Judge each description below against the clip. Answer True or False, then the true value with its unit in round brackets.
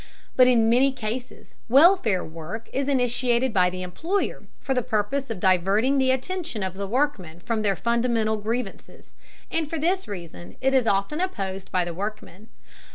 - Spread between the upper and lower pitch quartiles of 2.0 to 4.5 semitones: False (5.4 semitones)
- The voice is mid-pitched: False (230 Hz)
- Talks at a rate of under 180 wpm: True (165 wpm)